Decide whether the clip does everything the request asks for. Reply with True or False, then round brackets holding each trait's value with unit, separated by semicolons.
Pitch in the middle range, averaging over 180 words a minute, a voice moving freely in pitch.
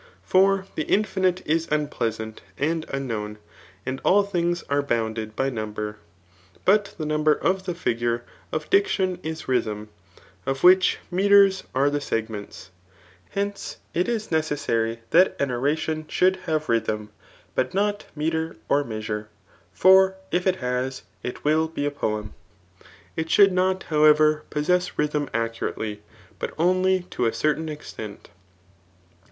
False (150 Hz; 135 wpm; 7.6 semitones)